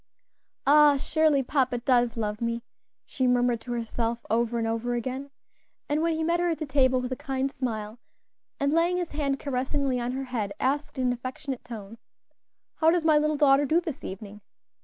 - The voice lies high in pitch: Yes, very high, 260 Hz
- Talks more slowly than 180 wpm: No, average, 190 wpm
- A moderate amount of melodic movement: Yes, average, 3.7 semitones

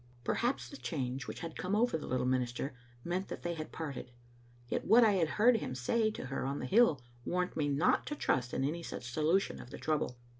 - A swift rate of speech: Yes, fast, 225 wpm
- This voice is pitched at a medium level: Yes, medium, 155 Hz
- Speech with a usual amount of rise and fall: No, wide, 7.0 semitones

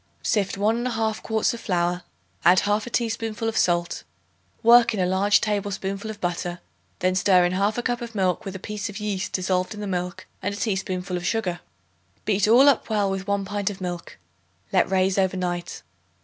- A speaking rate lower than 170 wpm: No, average, 190 wpm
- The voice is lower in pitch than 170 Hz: No, high, 195 Hz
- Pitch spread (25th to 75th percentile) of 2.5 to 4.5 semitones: Yes, average, 2.9 semitones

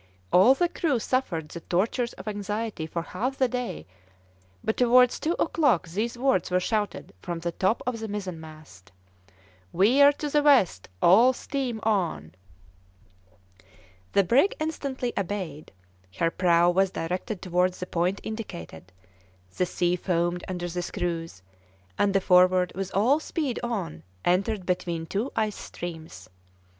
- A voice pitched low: No, high, 195 Hz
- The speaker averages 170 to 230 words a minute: No, average, 140 wpm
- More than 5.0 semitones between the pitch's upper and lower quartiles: Yes, wide, 5.5 semitones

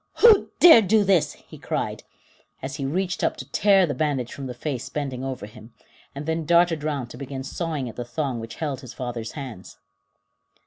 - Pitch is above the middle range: No, medium, 140 Hz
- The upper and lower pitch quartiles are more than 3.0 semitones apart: Yes, average, 4.8 semitones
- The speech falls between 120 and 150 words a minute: No, fast, 205 wpm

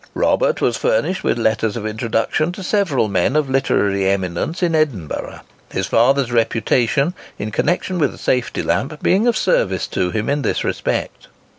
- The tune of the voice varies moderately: No, wide, 7.1 semitones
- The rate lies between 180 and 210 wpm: No, average, 165 wpm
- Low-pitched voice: Yes, low, 125 Hz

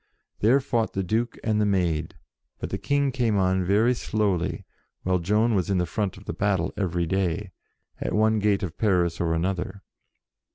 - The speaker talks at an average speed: Yes, average, 175 wpm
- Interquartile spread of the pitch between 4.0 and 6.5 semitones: No, average, 3.3 semitones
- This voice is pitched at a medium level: No, low, 100 Hz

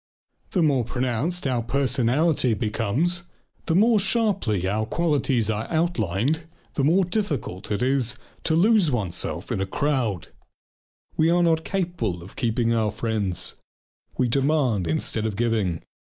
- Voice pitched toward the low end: Yes, low, 125 Hz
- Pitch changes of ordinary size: No, wide, 7.0 semitones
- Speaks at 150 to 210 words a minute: No, slow, 135 wpm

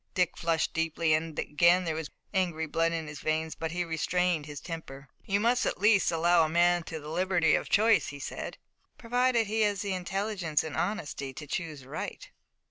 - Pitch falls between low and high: Yes, medium, 165 Hz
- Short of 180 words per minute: No, average, 195 wpm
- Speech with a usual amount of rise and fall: Yes, average, 3.1 semitones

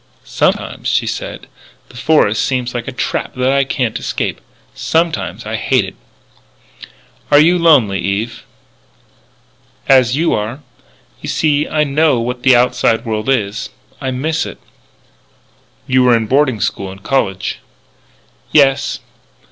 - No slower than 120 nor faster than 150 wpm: Yes, slow, 135 wpm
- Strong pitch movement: No, average, 4.2 semitones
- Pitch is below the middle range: Yes, low, 125 Hz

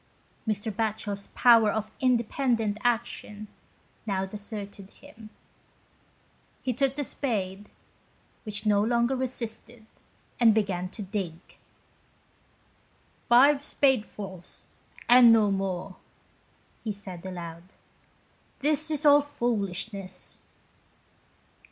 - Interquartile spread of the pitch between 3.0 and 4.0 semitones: Yes, average, 3.6 semitones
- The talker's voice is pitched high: Yes, high, 215 Hz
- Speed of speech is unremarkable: No, slow, 100 wpm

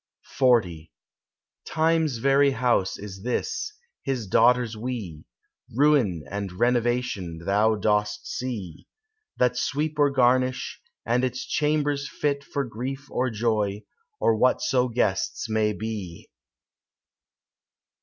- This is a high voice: No, low, 120 Hz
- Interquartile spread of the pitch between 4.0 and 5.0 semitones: Yes, average, 4.4 semitones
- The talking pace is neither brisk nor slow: No, slow, 105 wpm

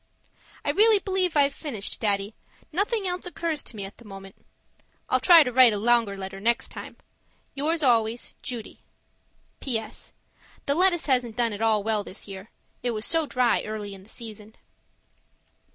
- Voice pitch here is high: Yes, high, 235 Hz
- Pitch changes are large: Yes, wide, 6.3 semitones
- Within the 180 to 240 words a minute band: No, average, 170 wpm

